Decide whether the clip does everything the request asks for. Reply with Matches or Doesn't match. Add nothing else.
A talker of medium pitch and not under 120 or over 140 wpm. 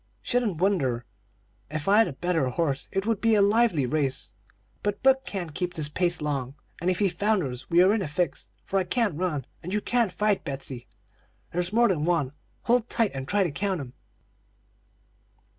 Doesn't match